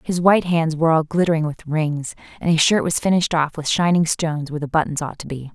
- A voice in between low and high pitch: Yes, medium, 160 Hz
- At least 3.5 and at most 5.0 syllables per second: No, 6.4 syllables/s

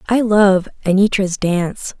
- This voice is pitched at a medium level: No, high, 195 Hz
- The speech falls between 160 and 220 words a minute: No, slow, 120 wpm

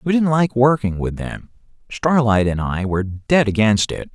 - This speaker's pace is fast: No, average, 190 wpm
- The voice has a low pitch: Yes, low, 115 Hz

